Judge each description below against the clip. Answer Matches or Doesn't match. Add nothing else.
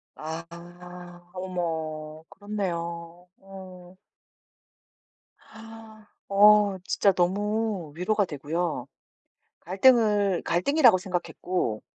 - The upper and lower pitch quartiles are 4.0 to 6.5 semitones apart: Doesn't match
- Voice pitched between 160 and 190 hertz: Matches